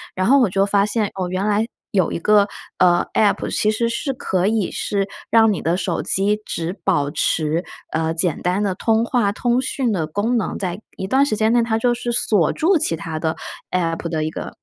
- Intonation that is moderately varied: Yes, average, 4.4 semitones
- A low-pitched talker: No, high, 200 Hz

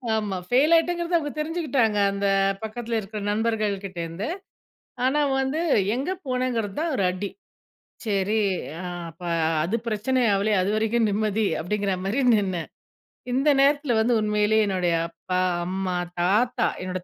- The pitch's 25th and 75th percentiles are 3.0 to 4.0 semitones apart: No, average, 4.6 semitones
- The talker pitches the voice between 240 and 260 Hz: No, high, 215 Hz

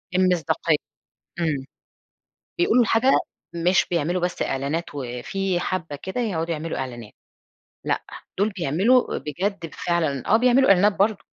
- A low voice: No, medium, 175 Hz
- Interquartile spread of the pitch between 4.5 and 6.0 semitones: Yes, average, 4.9 semitones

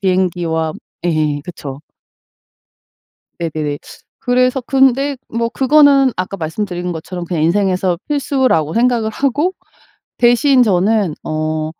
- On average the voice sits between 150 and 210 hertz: Yes, high, 190 Hz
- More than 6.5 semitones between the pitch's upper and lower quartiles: Yes, wide, 7.7 semitones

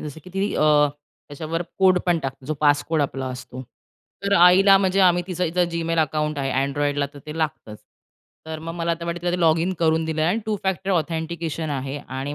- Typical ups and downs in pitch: Yes, average, 3.3 semitones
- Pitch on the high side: No, medium, 160 Hz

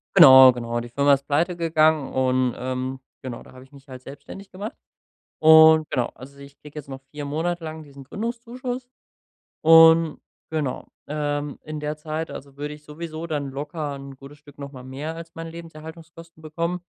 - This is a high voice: No, medium, 150 Hz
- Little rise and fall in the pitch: No, average, 3.0 semitones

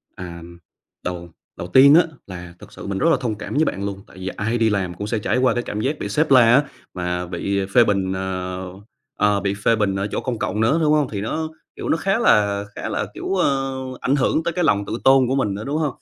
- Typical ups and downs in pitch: No, wide, 5.9 semitones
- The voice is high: No, low, 105 Hz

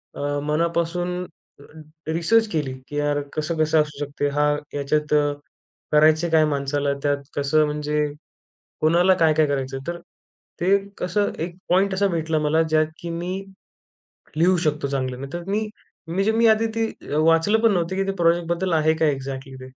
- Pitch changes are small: No, average, 3.1 semitones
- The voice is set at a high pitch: No, medium, 160 Hz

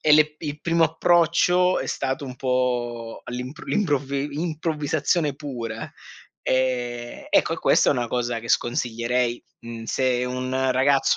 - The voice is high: No, low, 130 Hz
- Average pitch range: Yes, average, 3.8 semitones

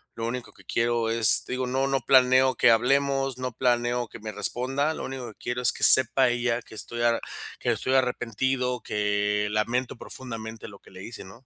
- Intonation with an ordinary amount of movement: No, narrow, 2.3 semitones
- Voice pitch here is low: Yes, low, 120 Hz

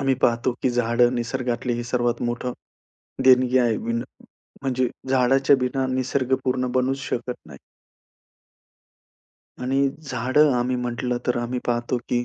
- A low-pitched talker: Yes, low, 125 Hz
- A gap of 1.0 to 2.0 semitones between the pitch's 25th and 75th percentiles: Yes, narrow, 1.3 semitones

